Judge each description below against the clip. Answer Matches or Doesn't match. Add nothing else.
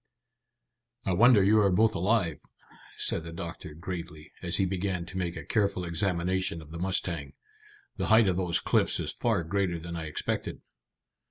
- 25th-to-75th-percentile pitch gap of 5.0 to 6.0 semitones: Doesn't match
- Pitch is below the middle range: Matches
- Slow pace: Doesn't match